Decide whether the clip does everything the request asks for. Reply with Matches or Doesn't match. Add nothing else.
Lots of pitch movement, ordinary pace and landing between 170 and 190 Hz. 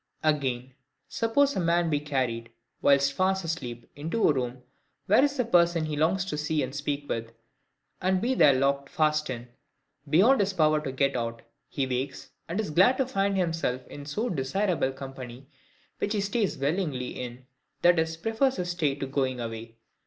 Doesn't match